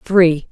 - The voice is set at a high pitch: No, medium, 170 Hz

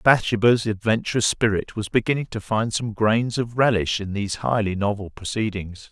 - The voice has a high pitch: No, low, 110 Hz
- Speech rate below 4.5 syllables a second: No, 5.2 syllables/s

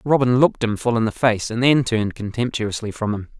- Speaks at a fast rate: Yes, fast, 230 wpm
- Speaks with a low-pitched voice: Yes, low, 115 Hz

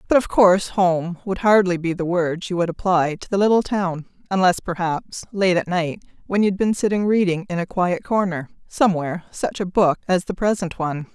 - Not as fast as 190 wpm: No, fast, 205 wpm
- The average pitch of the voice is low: No, medium, 185 Hz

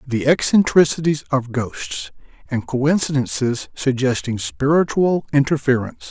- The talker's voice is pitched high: No, low, 130 Hz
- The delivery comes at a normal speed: No, slow, 90 wpm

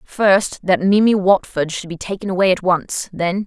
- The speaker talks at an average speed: Yes, average, 175 wpm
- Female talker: Yes, female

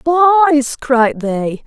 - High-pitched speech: Yes, very high, 275 Hz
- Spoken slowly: Yes, slow, 110 wpm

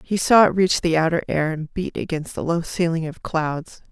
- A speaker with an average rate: No, fast, 230 wpm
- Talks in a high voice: No, medium, 170 Hz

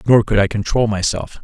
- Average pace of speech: No, fast, 210 wpm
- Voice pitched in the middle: No, low, 105 Hz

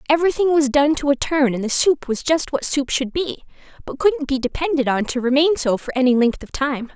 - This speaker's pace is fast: Yes, fast, 240 wpm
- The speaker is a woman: Yes, female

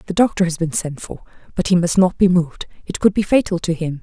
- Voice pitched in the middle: Yes, medium, 175 Hz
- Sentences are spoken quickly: Yes, fast, 270 wpm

